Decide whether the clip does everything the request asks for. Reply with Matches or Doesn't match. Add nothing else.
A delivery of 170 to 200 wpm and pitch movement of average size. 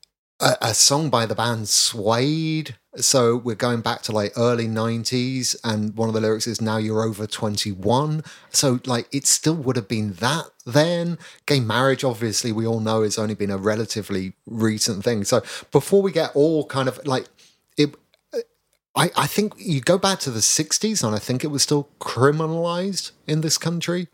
Doesn't match